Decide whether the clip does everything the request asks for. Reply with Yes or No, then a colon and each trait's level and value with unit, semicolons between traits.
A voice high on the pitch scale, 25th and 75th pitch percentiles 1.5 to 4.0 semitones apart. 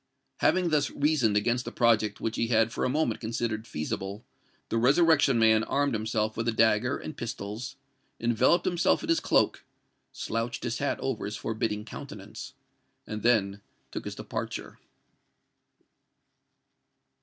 No: low, 115 Hz; average, 3.7 semitones